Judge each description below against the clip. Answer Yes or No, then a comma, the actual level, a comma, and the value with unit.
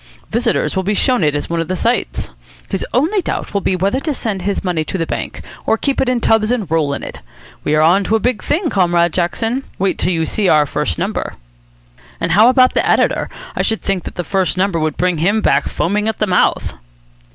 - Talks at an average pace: No, fast, 230 wpm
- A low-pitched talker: No, high, 195 Hz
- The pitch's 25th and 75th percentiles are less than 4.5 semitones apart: No, average, 4.8 semitones